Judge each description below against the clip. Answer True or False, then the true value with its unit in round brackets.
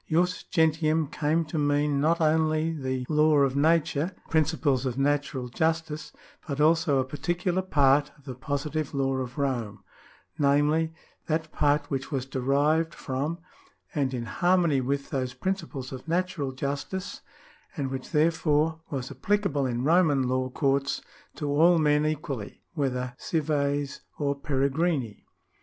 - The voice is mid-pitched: True (145 Hz)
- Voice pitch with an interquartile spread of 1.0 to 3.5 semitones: True (2.9 semitones)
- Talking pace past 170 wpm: False (145 wpm)